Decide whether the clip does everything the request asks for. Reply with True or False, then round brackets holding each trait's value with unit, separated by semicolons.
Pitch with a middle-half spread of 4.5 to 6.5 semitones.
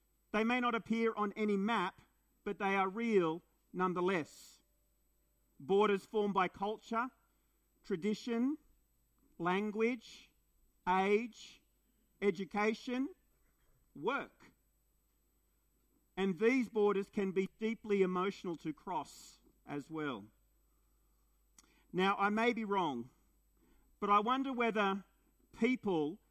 False (3.3 semitones)